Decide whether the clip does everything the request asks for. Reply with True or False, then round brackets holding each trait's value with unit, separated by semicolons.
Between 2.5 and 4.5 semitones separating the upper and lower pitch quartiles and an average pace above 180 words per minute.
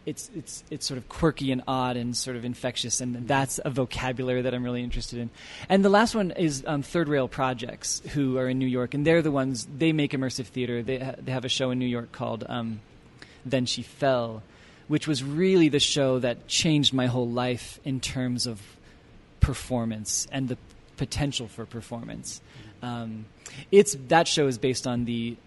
True (2.8 semitones; 200 wpm)